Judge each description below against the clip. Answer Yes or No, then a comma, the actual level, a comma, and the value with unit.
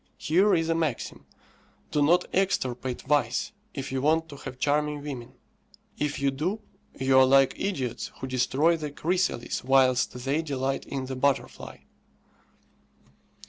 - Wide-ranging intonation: No, average, 3.3 semitones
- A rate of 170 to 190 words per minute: No, average, 140 wpm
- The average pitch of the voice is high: No, medium, 140 Hz